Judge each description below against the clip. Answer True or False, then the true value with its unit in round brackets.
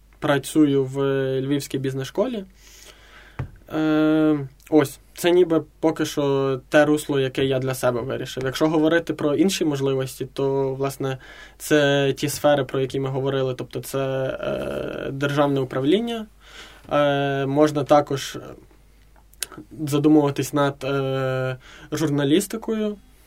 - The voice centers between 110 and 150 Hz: True (140 Hz)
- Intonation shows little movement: True (2.3 semitones)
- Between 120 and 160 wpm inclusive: False (105 wpm)